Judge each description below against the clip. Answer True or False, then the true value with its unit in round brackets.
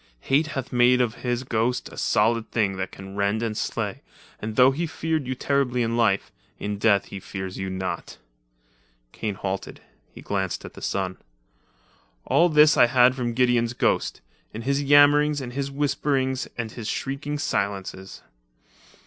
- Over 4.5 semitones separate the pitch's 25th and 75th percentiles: True (5.5 semitones)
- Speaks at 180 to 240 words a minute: False (170 wpm)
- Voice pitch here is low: True (120 Hz)